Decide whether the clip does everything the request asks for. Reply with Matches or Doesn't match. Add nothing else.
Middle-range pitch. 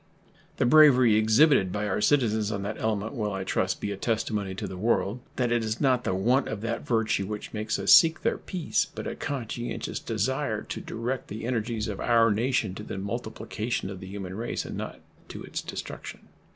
Doesn't match